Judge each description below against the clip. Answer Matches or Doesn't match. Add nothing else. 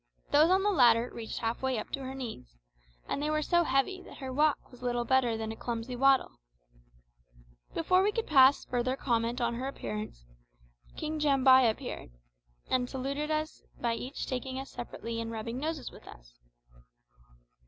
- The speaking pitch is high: Matches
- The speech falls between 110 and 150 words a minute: Doesn't match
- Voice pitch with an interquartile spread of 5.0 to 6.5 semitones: Doesn't match